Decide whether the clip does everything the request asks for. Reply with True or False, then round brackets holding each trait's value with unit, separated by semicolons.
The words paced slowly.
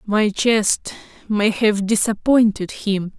True (115 wpm)